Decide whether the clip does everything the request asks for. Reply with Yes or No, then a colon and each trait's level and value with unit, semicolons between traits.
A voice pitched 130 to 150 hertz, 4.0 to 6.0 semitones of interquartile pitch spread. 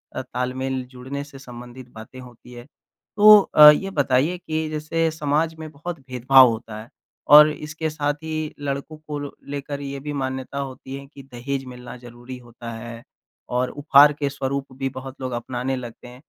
No: low, 135 Hz; average, 2.9 semitones